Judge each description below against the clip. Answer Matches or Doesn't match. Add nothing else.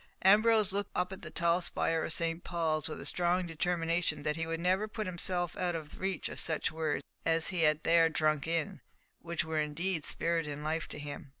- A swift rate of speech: Matches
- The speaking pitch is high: Doesn't match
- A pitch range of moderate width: Doesn't match